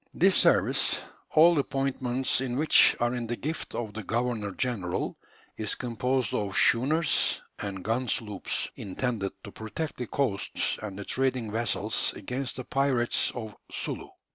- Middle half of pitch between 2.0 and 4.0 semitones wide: Yes, average, 3.7 semitones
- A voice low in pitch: Yes, low, 120 Hz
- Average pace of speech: Yes, average, 145 wpm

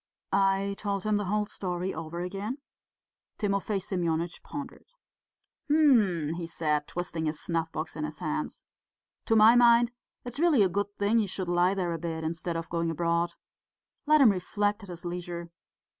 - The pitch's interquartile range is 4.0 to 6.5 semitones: No, average, 3.6 semitones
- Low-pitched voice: No, medium, 180 Hz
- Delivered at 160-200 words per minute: Yes, average, 170 wpm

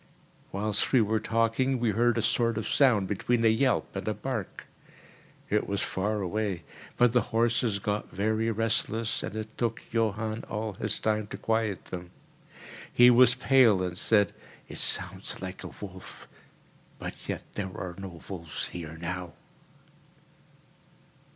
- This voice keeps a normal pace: Yes, average, 150 wpm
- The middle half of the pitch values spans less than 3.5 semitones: Yes, average, 2.8 semitones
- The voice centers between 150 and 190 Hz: No, low, 110 Hz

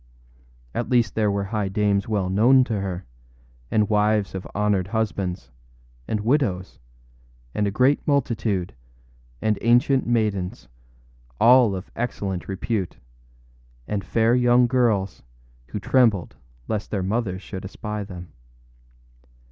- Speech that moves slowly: Yes, slow, 120 wpm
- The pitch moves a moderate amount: Yes, average, 3.4 semitones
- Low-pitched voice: Yes, low, 105 Hz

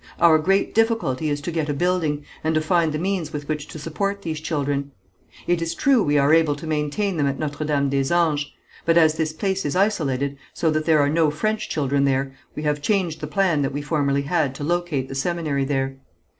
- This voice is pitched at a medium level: Yes, medium, 155 Hz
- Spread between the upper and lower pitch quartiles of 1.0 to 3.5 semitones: Yes, average, 3.0 semitones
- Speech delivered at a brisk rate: Yes, fast, 225 wpm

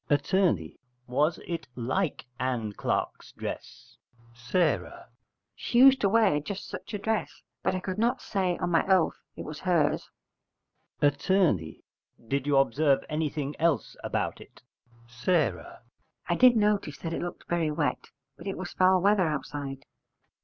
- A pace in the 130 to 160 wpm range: Yes, average, 145 wpm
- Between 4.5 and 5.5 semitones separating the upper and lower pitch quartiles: Yes, average, 5.2 semitones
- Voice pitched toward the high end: No, medium, 165 Hz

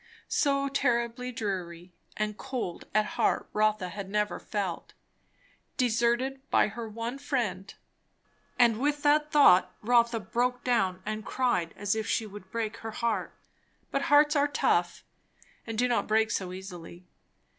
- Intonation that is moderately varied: Yes, average, 3.9 semitones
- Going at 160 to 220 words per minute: No, average, 145 wpm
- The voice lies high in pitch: Yes, high, 225 Hz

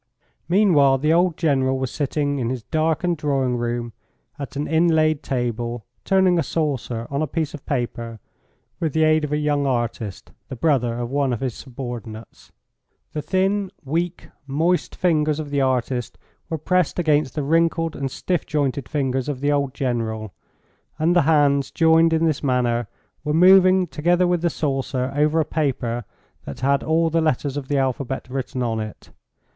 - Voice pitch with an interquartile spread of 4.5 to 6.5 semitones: No, average, 4.0 semitones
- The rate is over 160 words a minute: Yes, average, 175 wpm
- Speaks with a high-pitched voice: No, medium, 145 Hz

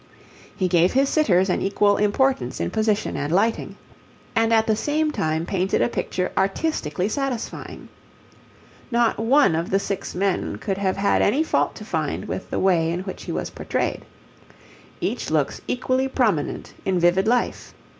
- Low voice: No, high, 200 Hz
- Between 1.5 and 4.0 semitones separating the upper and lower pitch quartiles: No, average, 4.7 semitones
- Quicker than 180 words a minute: No, average, 165 wpm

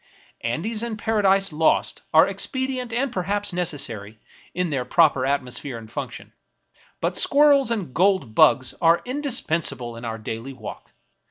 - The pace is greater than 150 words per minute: No, average, 140 wpm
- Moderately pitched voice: Yes, medium, 170 Hz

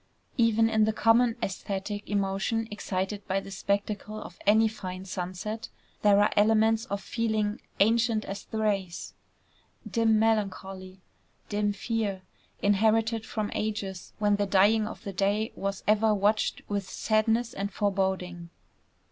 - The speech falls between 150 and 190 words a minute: No, slow, 135 wpm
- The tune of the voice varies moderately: No, narrow, 2.1 semitones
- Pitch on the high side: Yes, high, 210 Hz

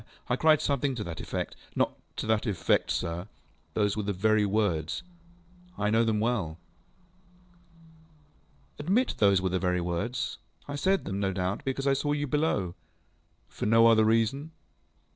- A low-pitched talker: Yes, low, 115 Hz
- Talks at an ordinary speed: Yes, average, 160 wpm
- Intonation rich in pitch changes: Yes, wide, 6.8 semitones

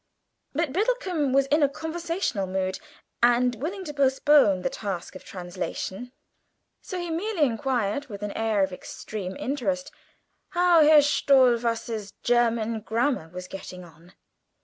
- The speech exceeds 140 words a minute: No, slow, 135 wpm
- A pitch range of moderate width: No, wide, 6.7 semitones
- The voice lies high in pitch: Yes, high, 245 Hz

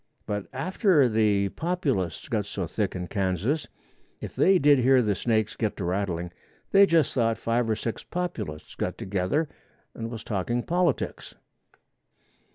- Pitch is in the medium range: No, low, 115 Hz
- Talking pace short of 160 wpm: Yes, average, 150 wpm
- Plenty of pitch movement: Yes, wide, 6.5 semitones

